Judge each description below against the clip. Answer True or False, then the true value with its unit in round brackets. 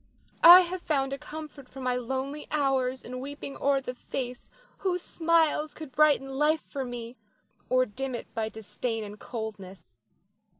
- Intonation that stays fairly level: False (3.4 semitones)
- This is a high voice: True (270 Hz)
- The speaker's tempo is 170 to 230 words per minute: False (160 wpm)